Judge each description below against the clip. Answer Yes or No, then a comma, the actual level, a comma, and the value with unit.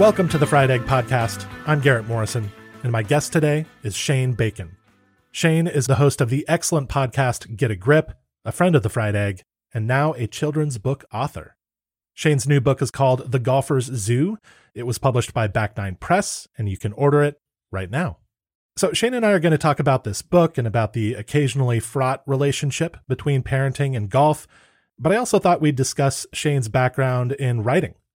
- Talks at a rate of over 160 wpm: Yes, average, 195 wpm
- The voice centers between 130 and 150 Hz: Yes, low, 135 Hz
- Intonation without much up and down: No, average, 4.4 semitones